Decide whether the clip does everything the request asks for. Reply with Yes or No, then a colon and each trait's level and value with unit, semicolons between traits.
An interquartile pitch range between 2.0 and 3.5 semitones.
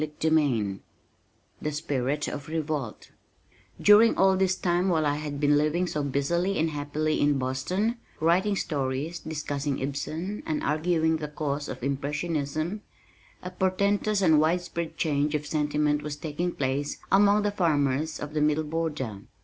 Yes: average, 3.1 semitones